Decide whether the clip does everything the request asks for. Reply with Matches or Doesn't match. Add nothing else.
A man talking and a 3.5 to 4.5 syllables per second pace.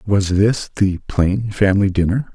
Matches